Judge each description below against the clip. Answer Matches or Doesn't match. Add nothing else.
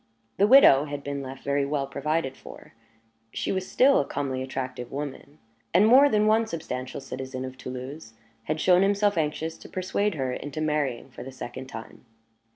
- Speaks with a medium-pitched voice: Matches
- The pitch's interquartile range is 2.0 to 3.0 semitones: Doesn't match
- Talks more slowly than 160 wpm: Doesn't match